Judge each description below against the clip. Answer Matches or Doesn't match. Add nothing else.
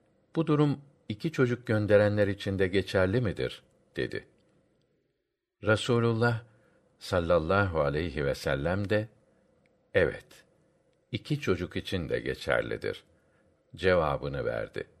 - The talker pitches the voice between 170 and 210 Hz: Doesn't match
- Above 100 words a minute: Doesn't match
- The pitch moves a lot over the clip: Matches